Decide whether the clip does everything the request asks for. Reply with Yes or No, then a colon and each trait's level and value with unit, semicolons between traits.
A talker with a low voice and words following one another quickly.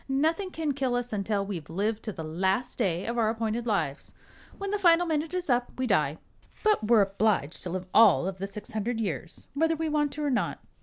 No: high, 225 Hz; fast, 220 wpm